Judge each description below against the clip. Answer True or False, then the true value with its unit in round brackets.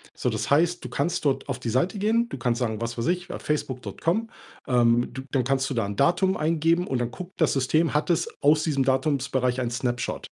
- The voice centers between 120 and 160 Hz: True (135 Hz)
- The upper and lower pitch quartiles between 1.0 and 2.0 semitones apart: False (5.3 semitones)